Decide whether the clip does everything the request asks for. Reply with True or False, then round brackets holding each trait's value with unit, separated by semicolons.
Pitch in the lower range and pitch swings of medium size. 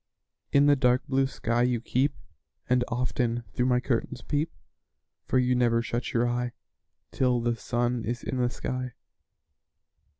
False (125 Hz; 1.2 semitones)